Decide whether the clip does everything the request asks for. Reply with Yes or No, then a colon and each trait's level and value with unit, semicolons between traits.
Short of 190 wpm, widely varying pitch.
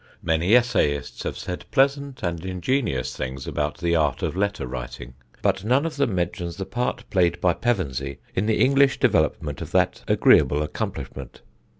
Yes: average, 165 wpm; wide, 8.8 semitones